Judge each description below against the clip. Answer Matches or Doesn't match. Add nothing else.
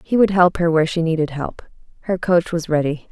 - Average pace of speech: Doesn't match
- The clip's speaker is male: Doesn't match